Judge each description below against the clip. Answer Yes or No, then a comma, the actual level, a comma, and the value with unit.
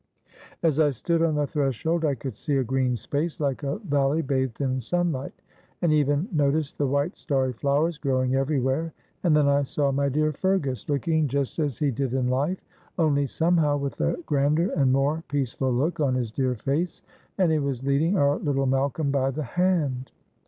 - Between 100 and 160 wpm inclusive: No, average, 190 wpm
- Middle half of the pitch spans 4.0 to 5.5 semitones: No, average, 2.7 semitones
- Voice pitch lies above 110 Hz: Yes, medium, 140 Hz